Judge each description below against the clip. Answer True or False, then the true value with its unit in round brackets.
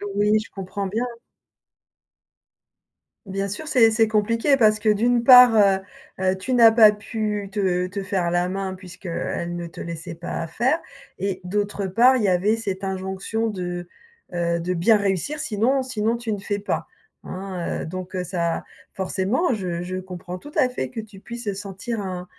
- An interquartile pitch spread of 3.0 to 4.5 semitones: True (3.4 semitones)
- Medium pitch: False (200 Hz)